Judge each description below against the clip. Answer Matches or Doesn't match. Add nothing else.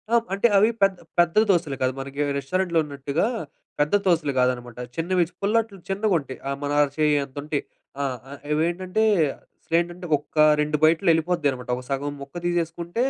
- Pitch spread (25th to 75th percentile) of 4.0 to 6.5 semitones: Matches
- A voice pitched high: Doesn't match